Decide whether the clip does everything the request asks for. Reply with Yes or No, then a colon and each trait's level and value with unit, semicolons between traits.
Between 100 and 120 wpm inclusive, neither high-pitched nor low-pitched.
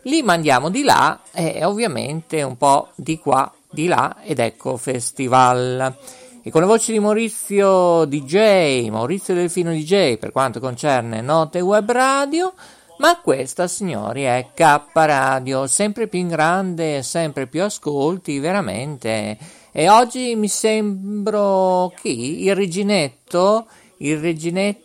No: average, 135 wpm; medium, 175 Hz